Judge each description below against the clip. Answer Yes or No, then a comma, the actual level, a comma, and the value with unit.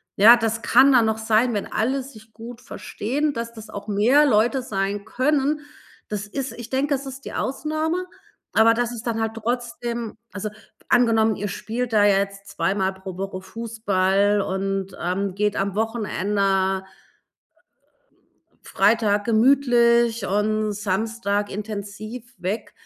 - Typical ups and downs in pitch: Yes, average, 3.1 semitones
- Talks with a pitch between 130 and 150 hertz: No, high, 220 Hz